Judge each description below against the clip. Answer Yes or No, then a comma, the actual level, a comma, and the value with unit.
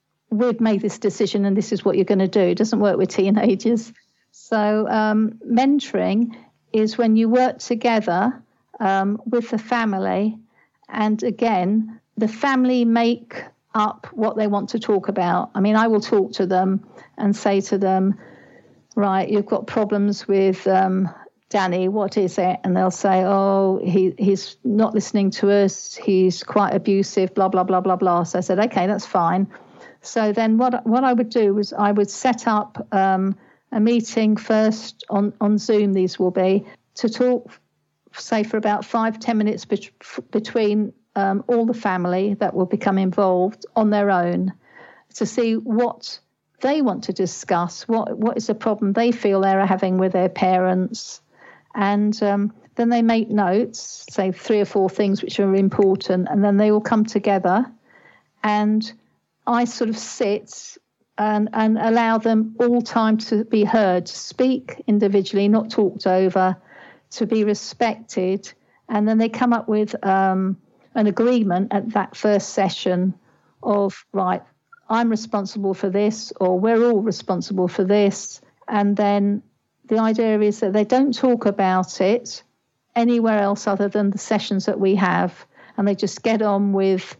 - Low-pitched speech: No, high, 210 Hz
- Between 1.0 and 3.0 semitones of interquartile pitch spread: Yes, narrow, 2.6 semitones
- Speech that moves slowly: No, average, 170 wpm